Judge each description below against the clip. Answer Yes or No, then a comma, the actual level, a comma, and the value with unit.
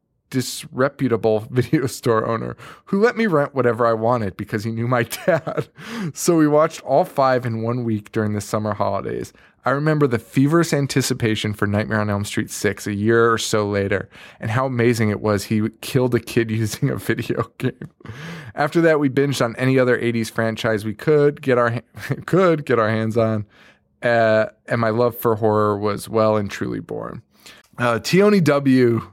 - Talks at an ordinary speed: Yes, average, 185 wpm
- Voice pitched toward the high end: No, low, 120 Hz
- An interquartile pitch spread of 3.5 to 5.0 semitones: Yes, average, 4.0 semitones